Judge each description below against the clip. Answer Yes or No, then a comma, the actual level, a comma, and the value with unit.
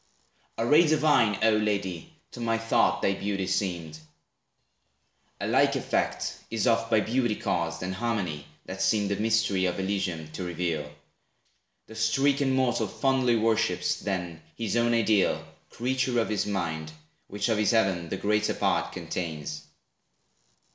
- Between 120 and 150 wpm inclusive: Yes, average, 145 wpm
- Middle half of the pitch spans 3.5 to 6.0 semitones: Yes, average, 4.2 semitones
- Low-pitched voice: Yes, low, 105 Hz